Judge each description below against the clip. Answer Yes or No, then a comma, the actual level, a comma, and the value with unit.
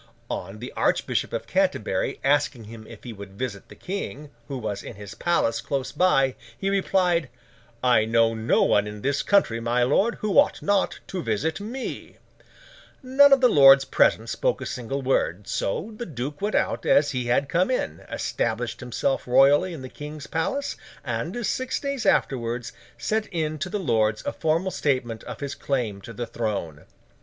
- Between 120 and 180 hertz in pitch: Yes, low, 135 Hz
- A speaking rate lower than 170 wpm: No, average, 180 wpm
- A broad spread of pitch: Yes, wide, 7.7 semitones